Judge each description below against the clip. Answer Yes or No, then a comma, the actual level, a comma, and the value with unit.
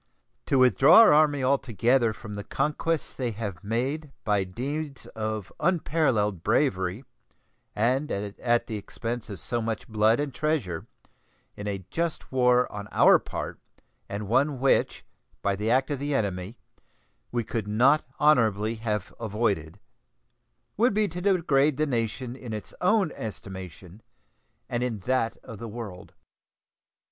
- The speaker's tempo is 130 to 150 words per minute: Yes, average, 140 wpm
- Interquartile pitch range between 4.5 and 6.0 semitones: Yes, average, 5.1 semitones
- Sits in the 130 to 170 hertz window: No, low, 120 Hz